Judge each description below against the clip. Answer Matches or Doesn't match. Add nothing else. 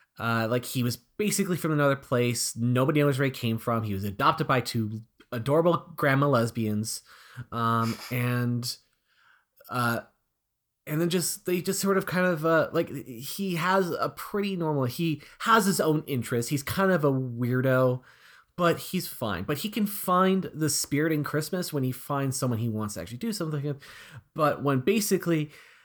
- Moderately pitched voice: Matches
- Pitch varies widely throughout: Matches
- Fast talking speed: Doesn't match